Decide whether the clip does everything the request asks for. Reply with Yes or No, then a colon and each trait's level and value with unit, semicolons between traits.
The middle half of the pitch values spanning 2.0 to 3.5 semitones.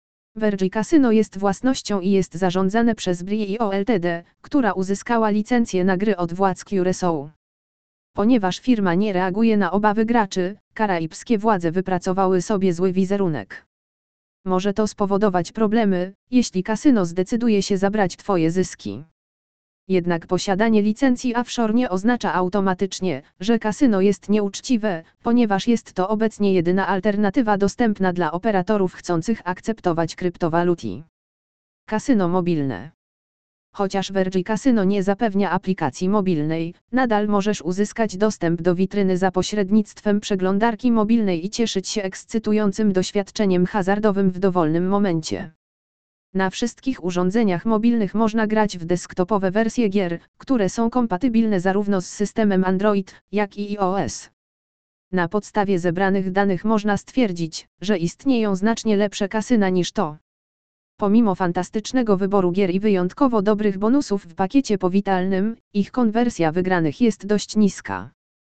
Yes: average, 2.9 semitones